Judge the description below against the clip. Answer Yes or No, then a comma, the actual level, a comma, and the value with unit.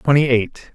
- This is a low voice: Yes, low, 130 Hz